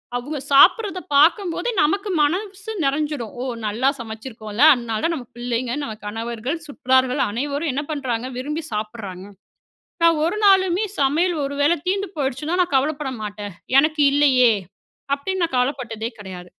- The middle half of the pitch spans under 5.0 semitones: No, wide, 5.5 semitones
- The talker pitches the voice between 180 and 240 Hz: No, very high, 275 Hz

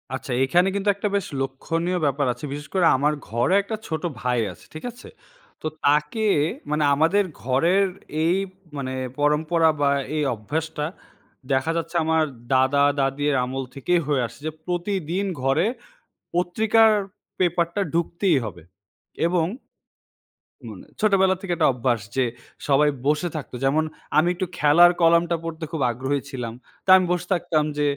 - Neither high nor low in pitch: Yes, medium, 155 Hz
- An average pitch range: Yes, average, 4.1 semitones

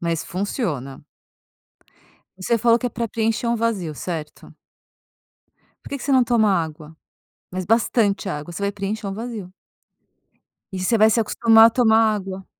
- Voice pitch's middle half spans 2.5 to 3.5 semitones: No, average, 4.1 semitones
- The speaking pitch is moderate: No, high, 210 Hz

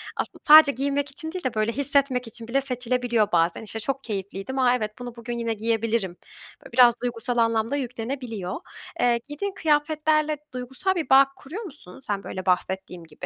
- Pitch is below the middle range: No, high, 245 Hz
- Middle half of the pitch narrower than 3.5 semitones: No, average, 3.9 semitones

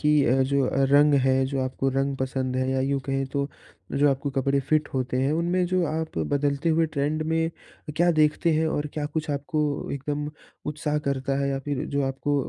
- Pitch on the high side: No, medium, 140 Hz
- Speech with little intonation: Yes, narrow, 2.1 semitones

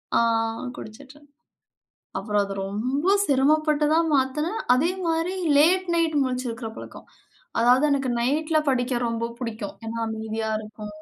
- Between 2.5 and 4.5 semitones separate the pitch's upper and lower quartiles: No, average, 5.3 semitones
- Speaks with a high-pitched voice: Yes, very high, 260 Hz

